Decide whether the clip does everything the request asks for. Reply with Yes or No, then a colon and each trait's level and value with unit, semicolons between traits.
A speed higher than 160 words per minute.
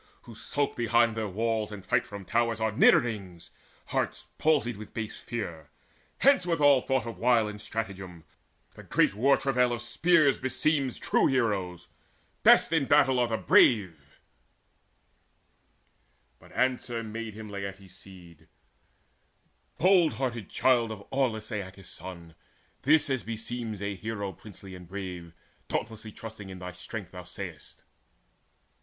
No: average, 145 wpm